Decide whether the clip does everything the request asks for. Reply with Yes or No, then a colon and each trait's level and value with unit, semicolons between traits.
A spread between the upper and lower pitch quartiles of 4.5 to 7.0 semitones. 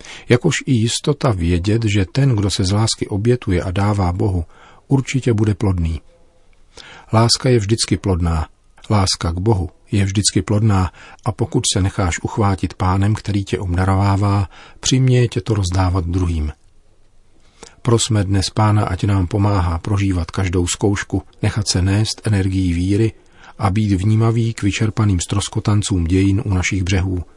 No: average, 2.9 semitones